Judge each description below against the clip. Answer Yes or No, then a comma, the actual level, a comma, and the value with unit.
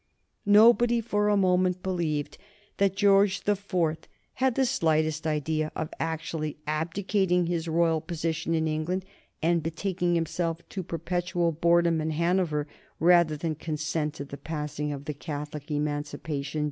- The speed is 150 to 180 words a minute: No, slow, 135 wpm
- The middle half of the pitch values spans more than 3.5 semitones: No, average, 2.8 semitones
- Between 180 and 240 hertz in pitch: No, medium, 165 Hz